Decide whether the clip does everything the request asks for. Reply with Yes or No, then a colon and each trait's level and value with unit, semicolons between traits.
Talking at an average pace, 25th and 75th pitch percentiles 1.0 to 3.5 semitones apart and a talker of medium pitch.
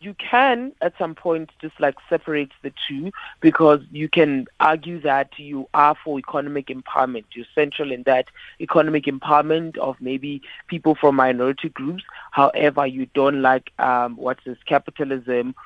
Yes: average, 155 wpm; average, 3.1 semitones; medium, 145 Hz